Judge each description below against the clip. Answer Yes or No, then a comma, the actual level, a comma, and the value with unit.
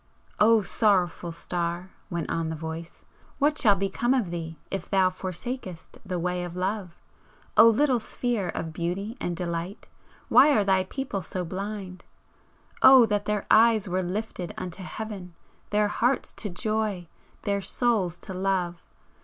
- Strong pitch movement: No, average, 3.6 semitones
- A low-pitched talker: No, high, 190 Hz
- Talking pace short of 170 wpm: Yes, average, 150 wpm